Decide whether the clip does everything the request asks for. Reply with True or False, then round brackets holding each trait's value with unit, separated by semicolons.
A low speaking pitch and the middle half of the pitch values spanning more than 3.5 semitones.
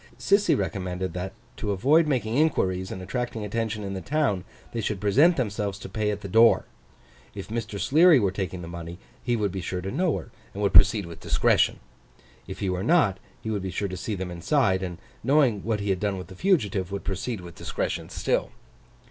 True (100 Hz; 3.9 semitones)